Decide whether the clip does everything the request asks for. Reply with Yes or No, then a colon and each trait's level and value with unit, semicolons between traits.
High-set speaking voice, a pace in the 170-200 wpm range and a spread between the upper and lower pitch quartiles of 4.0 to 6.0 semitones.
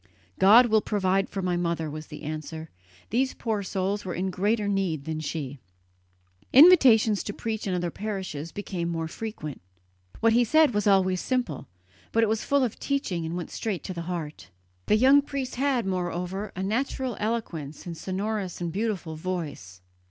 Yes: high, 195 Hz; average, 175 wpm; average, 4.8 semitones